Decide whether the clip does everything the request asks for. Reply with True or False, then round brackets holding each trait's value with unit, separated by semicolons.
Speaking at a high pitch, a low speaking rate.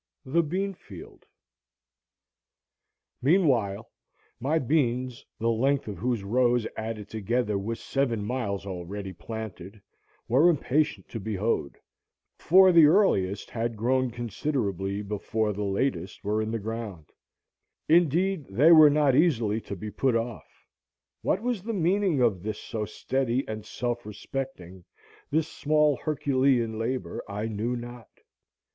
False (120 Hz; 130 wpm)